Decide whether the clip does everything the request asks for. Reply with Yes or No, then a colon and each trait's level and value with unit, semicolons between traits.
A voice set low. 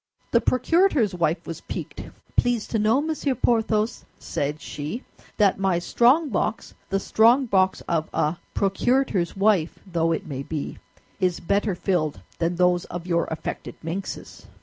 No: high, 195 Hz